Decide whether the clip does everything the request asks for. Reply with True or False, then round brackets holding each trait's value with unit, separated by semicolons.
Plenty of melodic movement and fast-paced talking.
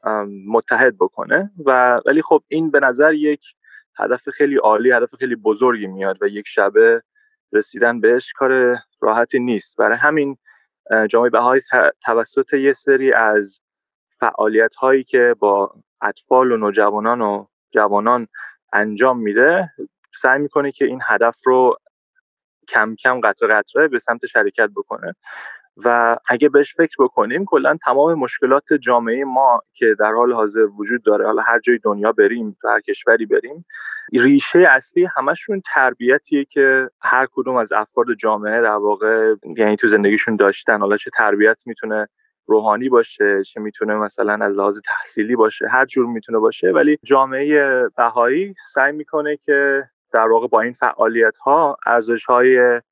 False (6.8 semitones; 145 wpm)